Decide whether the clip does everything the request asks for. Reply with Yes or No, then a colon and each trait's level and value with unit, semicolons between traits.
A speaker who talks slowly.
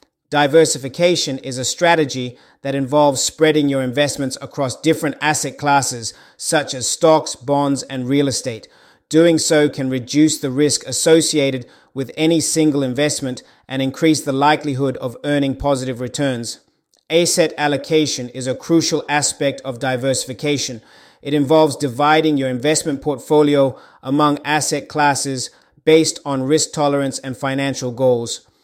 Yes: slow, 130 wpm